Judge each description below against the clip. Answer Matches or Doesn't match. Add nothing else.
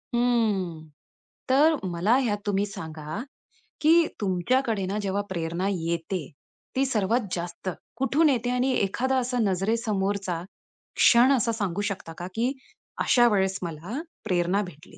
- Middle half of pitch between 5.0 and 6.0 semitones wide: Matches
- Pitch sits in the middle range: Doesn't match